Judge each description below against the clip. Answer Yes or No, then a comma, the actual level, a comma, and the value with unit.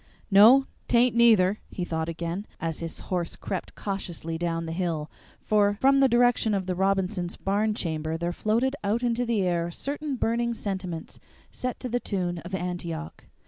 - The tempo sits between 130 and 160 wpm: No, average, 175 wpm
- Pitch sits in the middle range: No, high, 195 Hz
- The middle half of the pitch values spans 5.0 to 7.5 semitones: Yes, average, 5.3 semitones